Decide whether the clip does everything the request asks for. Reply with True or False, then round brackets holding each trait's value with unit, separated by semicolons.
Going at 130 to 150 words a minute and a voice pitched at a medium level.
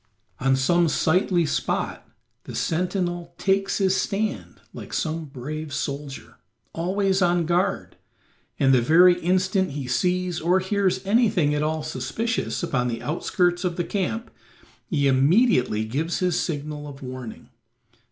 True (135 wpm; 170 Hz)